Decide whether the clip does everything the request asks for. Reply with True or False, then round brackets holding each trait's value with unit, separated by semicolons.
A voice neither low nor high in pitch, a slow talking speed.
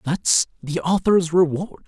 True (165 Hz; 130 wpm)